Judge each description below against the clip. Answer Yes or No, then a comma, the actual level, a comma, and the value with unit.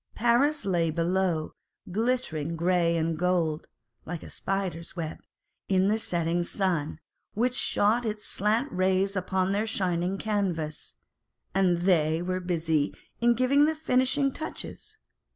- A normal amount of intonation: Yes, average, 4.7 semitones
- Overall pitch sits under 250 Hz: Yes, medium, 185 Hz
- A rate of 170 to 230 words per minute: No, slow, 135 wpm